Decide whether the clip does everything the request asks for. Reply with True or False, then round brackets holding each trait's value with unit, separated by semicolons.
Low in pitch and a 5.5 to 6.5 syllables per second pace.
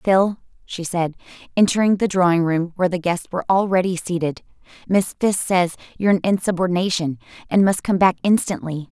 False (180 Hz; 5.8 syllables/s)